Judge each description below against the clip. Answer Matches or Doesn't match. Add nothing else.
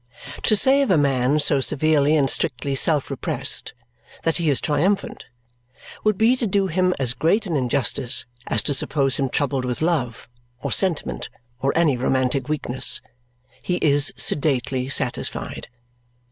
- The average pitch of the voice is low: Doesn't match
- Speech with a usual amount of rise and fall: Matches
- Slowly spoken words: Doesn't match